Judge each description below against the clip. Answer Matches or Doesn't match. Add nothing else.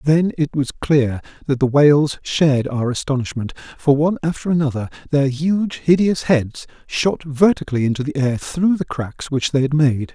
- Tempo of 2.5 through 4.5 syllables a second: Doesn't match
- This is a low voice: Doesn't match